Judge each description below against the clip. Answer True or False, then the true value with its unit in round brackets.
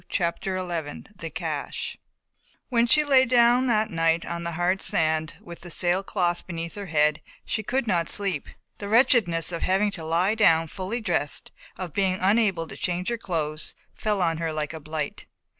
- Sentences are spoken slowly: False (175 wpm)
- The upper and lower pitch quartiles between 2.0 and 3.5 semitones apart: False (4.3 semitones)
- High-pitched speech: False (175 Hz)